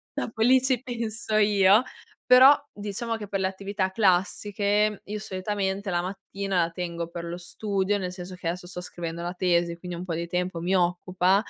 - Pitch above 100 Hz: Yes, high, 190 Hz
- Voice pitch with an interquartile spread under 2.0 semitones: No, narrow, 2.6 semitones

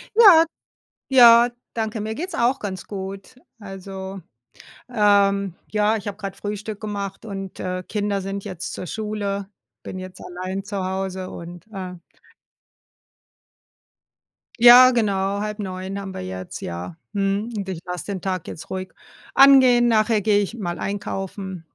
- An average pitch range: No, narrow, 2.3 semitones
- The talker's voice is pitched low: No, high, 200 Hz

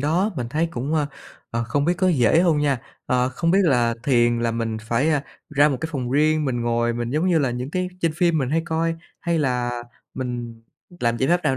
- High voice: No, medium, 140 Hz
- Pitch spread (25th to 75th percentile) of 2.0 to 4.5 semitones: No, average, 5.1 semitones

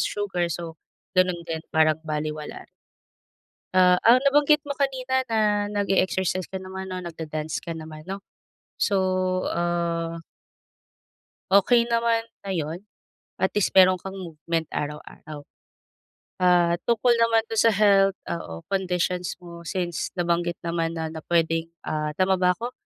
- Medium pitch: Yes, medium, 180 Hz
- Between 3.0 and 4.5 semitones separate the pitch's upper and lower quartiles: Yes, average, 3.6 semitones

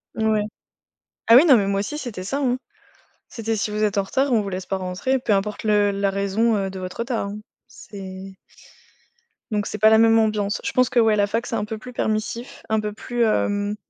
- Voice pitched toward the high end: Yes, high, 215 Hz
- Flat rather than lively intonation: Yes, narrow, 2.3 semitones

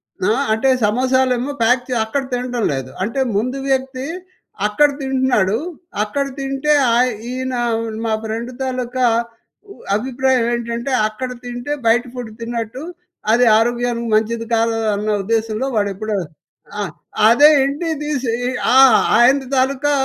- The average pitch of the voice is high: Yes, high, 245 Hz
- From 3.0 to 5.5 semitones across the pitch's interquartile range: No, narrow, 2.6 semitones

